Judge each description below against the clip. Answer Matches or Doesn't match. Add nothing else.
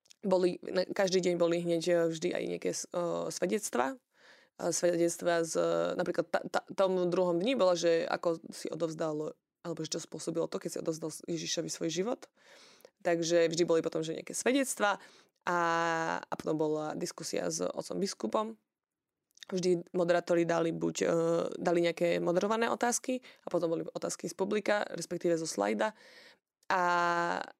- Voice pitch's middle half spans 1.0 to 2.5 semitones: Matches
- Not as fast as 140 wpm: Doesn't match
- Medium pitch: Matches